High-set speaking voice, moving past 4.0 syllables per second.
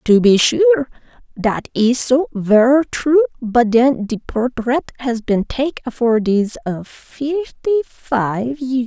No: very high, 250 Hz; 3.5 syllables/s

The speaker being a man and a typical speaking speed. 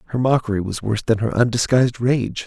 Yes: male; average, 195 wpm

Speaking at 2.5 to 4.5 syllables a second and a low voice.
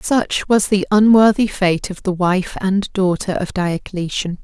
No: 4.0 syllables/s; high, 190 Hz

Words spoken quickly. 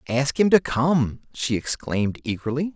No: average, 155 wpm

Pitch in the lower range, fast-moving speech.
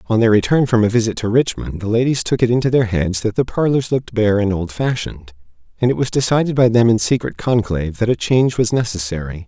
Yes: low, 110 Hz; fast, 230 wpm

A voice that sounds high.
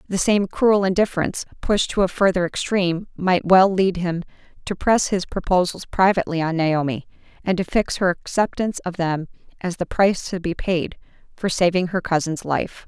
No: medium, 180 Hz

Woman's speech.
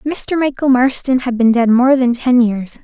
Yes: female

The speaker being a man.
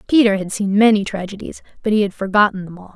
No: female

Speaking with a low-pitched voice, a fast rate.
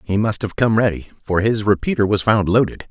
Yes: low, 105 Hz; fast, 225 wpm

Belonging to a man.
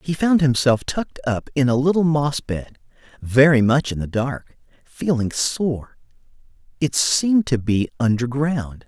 Yes: male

